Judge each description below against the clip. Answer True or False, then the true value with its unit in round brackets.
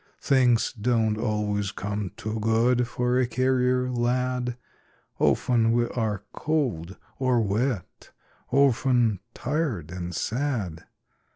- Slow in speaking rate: True (105 wpm)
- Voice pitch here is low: True (120 Hz)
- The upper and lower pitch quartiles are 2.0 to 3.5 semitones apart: True (3.2 semitones)